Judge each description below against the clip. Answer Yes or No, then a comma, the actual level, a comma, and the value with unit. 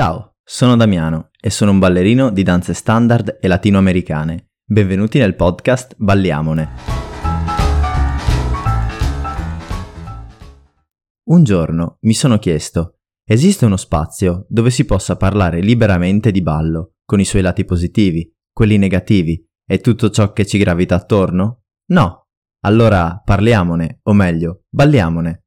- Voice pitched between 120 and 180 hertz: No, very low, 95 Hz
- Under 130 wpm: Yes, average, 120 wpm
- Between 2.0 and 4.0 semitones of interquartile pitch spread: No, average, 4.7 semitones